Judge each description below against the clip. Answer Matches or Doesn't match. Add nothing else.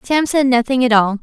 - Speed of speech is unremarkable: Doesn't match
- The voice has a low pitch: Doesn't match